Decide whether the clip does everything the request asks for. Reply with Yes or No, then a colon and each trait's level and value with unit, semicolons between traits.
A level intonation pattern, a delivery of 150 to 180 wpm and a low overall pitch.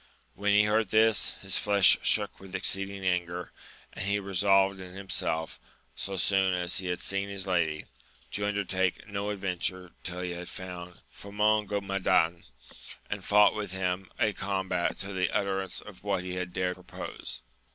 Yes: narrow, 1.8 semitones; average, 160 wpm; very low, 95 Hz